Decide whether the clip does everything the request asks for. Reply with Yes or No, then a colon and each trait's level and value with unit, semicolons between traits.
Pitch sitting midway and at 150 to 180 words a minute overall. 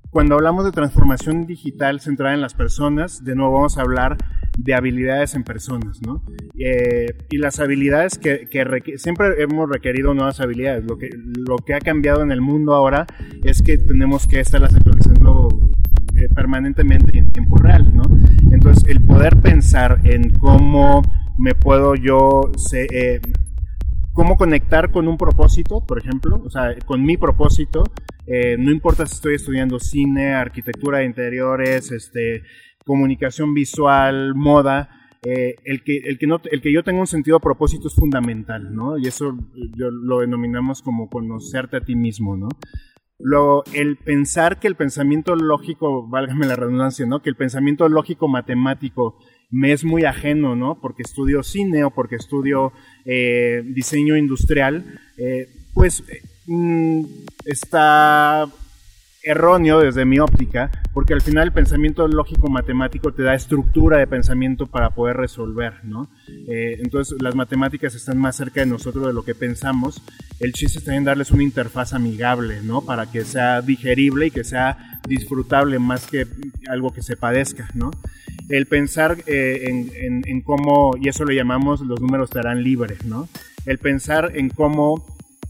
No: low, 130 Hz; average, 160 wpm